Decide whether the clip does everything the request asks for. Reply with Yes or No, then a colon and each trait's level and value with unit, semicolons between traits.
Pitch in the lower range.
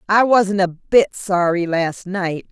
No: high, 190 Hz